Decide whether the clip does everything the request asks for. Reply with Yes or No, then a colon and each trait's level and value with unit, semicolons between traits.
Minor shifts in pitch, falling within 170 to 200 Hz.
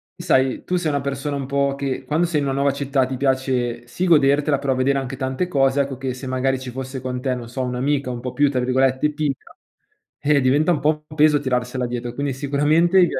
No: narrow, 2.0 semitones; low, 135 Hz